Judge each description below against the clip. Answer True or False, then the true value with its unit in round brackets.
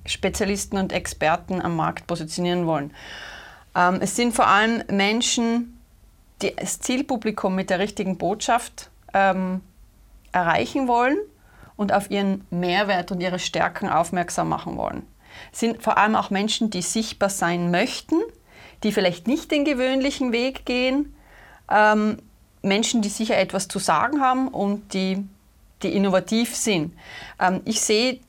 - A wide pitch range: False (4.3 semitones)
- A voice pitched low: False (200 Hz)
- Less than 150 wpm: True (140 wpm)